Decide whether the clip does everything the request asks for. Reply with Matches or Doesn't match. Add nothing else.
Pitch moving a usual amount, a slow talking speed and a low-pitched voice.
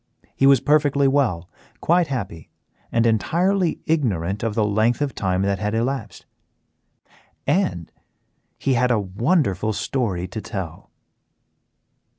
Doesn't match